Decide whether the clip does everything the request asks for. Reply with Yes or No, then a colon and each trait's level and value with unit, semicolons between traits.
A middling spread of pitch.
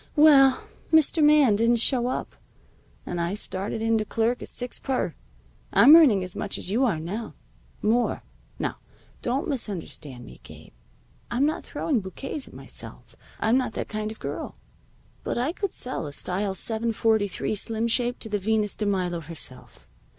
Yes: average, 4.4 semitones